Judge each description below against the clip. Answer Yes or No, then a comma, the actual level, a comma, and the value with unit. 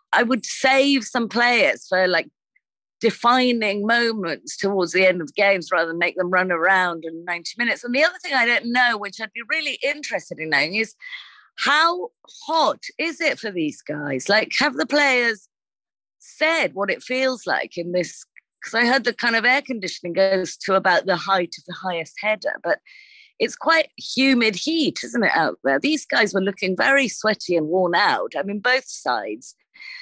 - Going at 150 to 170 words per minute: No, average, 190 wpm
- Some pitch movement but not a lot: No, wide, 7.6 semitones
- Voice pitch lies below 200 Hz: No, high, 230 Hz